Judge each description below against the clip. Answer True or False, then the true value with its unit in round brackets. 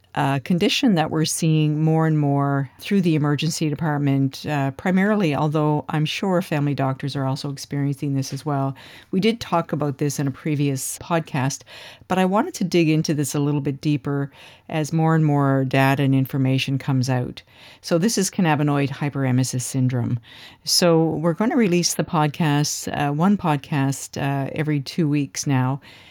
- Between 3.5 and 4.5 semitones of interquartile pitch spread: False (3.0 semitones)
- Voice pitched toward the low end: False (145 Hz)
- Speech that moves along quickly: False (170 wpm)